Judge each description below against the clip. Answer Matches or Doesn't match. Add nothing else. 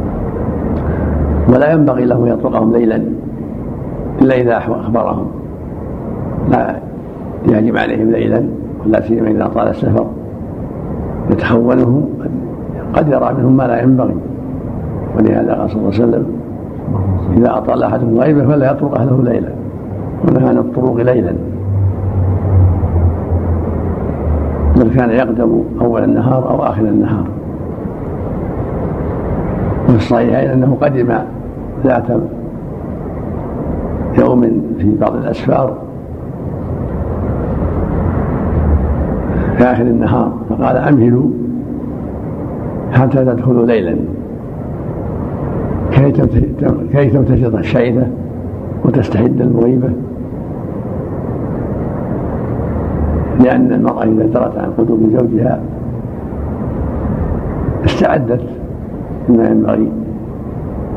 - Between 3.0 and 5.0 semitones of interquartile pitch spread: Doesn't match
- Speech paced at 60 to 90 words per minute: Matches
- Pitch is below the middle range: Matches